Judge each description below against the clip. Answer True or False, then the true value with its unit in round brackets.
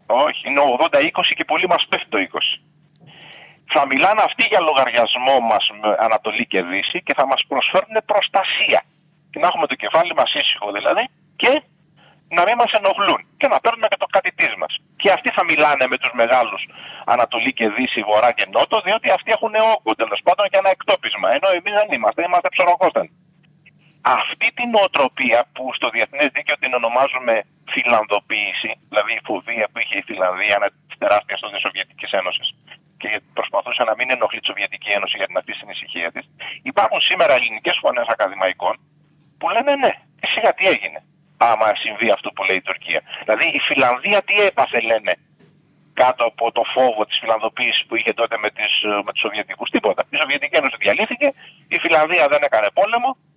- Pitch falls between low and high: True (165 Hz)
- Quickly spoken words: True (175 wpm)